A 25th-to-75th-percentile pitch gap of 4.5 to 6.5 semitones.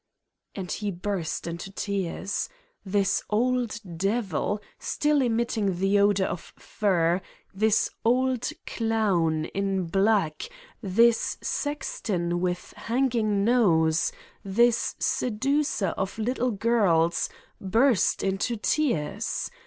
No: average, 4.1 semitones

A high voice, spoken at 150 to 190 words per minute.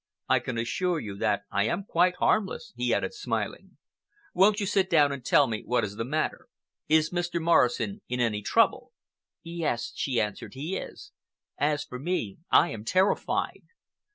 No: medium, 150 Hz; average, 170 wpm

